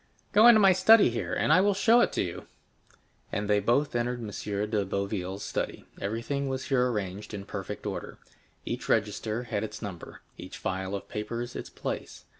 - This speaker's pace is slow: No, average, 185 wpm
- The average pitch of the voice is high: No, low, 110 Hz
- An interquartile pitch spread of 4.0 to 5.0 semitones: Yes, average, 4.7 semitones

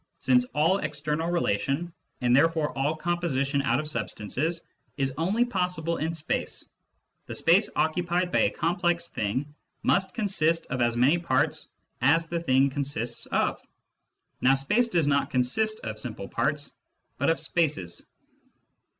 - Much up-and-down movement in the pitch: No, average, 4.4 semitones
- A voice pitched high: No, medium, 150 Hz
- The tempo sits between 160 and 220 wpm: No, average, 140 wpm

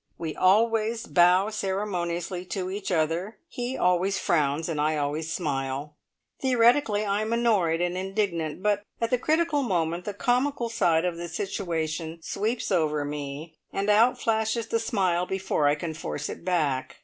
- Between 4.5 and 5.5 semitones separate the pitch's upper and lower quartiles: Yes, average, 5.2 semitones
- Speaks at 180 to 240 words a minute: No, average, 160 wpm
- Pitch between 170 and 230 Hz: Yes, medium, 185 Hz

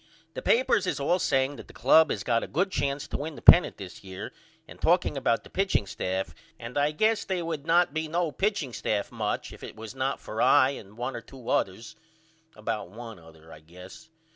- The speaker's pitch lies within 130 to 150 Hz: Yes, low, 135 Hz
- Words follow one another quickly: Yes, fast, 215 wpm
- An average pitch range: No, wide, 7.0 semitones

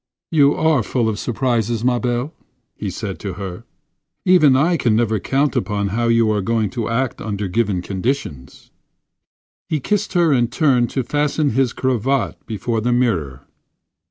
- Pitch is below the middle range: Yes, low, 120 Hz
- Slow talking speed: No, average, 160 wpm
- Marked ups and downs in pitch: No, average, 4.4 semitones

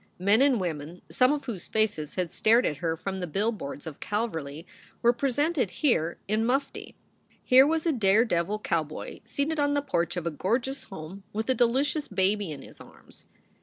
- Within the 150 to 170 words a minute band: No, average, 185 wpm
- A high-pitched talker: Yes, high, 210 Hz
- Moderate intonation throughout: No, wide, 7.2 semitones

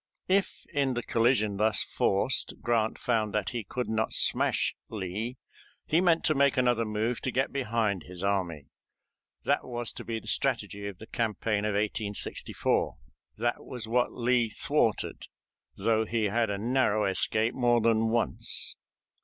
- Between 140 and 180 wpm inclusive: Yes, average, 155 wpm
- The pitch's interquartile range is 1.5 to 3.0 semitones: Yes, narrow, 2.6 semitones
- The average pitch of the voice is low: Yes, low, 115 Hz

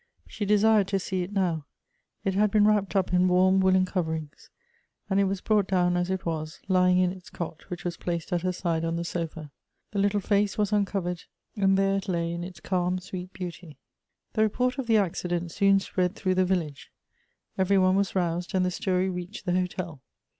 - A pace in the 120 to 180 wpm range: No, fast, 205 wpm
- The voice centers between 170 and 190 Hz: Yes, medium, 185 Hz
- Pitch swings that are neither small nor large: No, narrow, 1.9 semitones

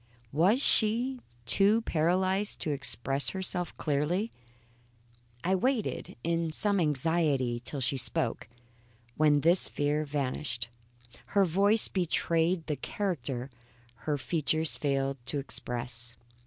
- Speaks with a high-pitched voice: No, medium, 155 Hz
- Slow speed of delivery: Yes, slow, 110 wpm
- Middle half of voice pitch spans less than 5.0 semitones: No, wide, 5.4 semitones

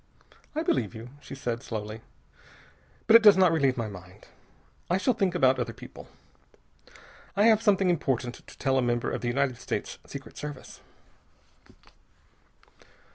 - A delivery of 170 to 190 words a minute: No, average, 150 wpm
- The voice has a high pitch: No, low, 135 Hz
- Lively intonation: Yes, wide, 7.5 semitones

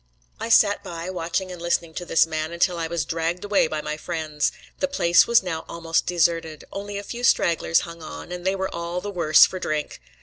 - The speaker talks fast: Yes, fast, 215 wpm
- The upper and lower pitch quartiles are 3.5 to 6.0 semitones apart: No, narrow, 2.4 semitones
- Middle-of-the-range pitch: Yes, medium, 170 Hz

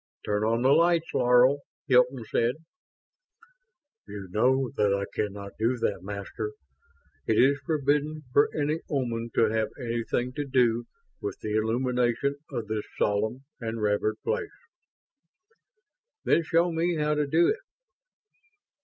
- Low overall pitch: Yes, low, 125 Hz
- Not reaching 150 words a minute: Yes, slow, 135 wpm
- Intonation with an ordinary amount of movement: Yes, average, 4.8 semitones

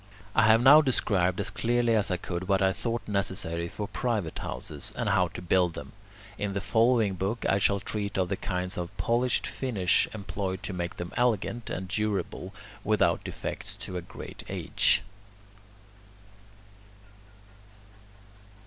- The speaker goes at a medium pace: Yes, average, 150 wpm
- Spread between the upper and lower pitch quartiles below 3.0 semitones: No, average, 3.5 semitones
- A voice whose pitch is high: No, low, 100 Hz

